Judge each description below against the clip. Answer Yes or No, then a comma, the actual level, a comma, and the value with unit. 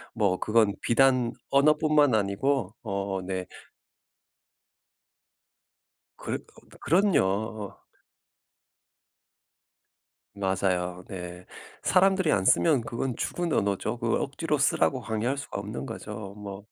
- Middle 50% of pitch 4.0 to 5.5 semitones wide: No, wide, 5.9 semitones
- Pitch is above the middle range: No, low, 110 Hz